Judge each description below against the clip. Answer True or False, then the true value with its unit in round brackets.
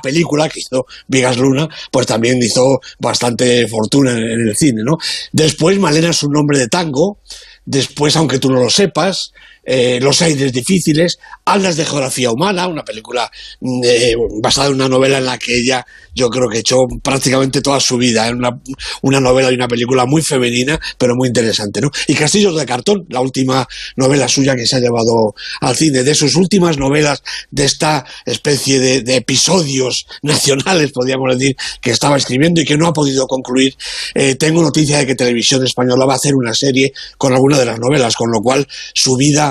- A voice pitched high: False (135 Hz)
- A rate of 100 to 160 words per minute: False (190 wpm)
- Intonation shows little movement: False (3.0 semitones)